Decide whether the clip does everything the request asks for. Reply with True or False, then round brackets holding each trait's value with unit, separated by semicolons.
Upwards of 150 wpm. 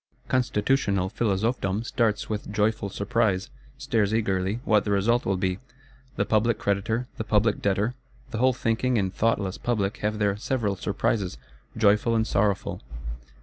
False (145 wpm)